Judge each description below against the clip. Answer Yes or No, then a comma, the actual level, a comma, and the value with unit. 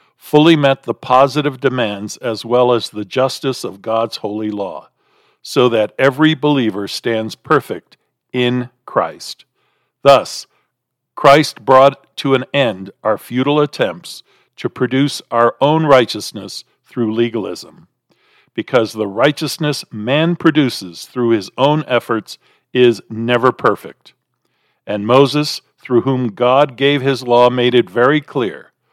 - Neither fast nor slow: No, slow, 130 wpm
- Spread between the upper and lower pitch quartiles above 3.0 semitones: Yes, average, 3.4 semitones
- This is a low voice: Yes, low, 125 Hz